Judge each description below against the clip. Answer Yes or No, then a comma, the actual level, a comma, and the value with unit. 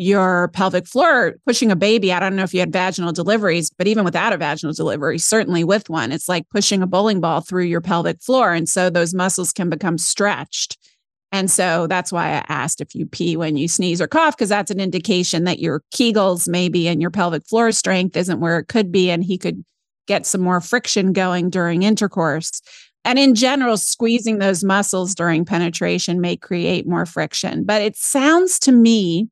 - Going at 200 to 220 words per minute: Yes, fast, 205 wpm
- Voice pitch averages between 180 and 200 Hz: Yes, medium, 185 Hz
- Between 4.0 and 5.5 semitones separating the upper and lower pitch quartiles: No, average, 3.4 semitones